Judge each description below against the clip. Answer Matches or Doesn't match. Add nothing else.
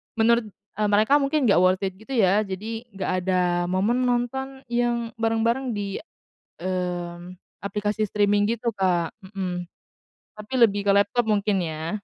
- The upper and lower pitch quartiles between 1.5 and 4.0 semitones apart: Matches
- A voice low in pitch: Doesn't match